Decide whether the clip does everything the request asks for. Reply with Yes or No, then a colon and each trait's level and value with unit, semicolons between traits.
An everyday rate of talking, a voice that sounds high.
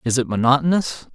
No: average, 155 wpm; low, 135 Hz